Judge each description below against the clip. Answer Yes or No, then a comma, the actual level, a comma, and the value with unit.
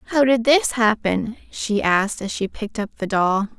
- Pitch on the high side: Yes, high, 220 Hz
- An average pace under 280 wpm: Yes, average, 200 wpm